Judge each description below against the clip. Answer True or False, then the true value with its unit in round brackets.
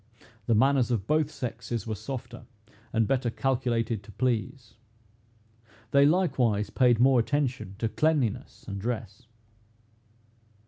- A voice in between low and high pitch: False (120 Hz)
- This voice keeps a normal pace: False (120 wpm)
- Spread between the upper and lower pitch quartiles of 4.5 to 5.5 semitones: False (3.1 semitones)